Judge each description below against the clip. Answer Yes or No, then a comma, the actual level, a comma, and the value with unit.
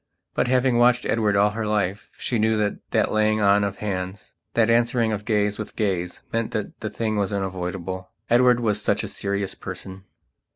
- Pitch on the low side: Yes, low, 105 Hz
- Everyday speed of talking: Yes, average, 190 wpm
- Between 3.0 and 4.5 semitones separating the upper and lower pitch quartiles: No, narrow, 2.4 semitones